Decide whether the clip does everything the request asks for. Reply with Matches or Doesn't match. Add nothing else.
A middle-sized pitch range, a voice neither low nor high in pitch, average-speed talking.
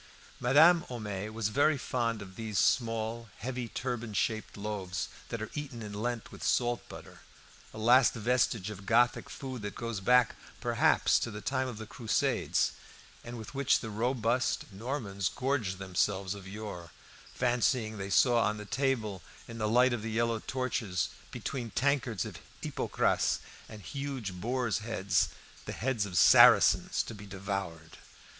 Doesn't match